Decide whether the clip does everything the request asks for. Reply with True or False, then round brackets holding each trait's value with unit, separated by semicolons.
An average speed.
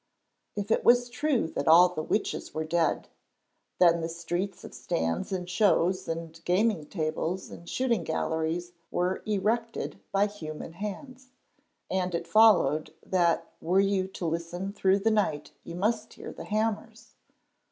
True (150 wpm)